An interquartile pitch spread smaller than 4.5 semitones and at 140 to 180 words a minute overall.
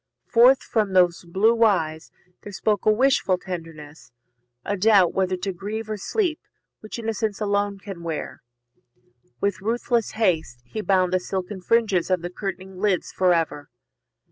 Yes: average, 3.3 semitones; average, 150 wpm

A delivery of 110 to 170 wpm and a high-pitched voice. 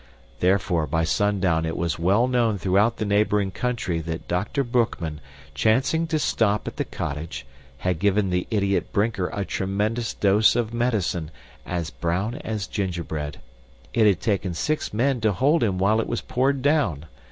No: average, 165 wpm; low, 100 Hz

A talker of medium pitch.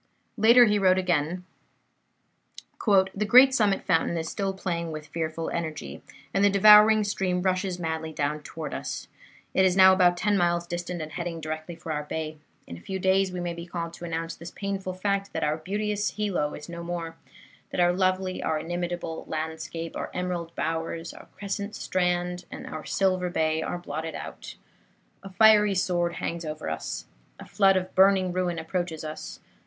Yes: medium, 175 Hz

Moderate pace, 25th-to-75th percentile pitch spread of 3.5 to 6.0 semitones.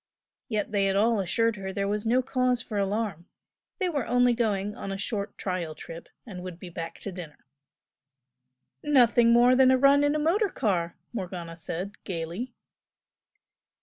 Yes: average, 170 wpm; average, 5.1 semitones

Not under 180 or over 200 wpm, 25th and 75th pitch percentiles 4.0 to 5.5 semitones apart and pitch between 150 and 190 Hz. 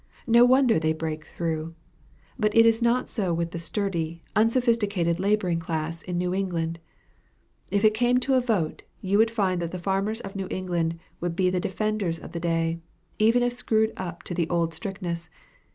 Yes: average, 185 wpm; average, 4.5 semitones; medium, 185 Hz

